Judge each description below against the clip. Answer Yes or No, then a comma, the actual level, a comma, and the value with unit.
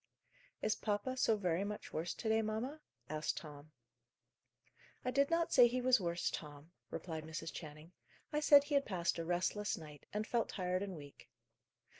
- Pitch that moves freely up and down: Yes, wide, 7.1 semitones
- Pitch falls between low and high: No, high, 195 Hz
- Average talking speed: Yes, average, 175 wpm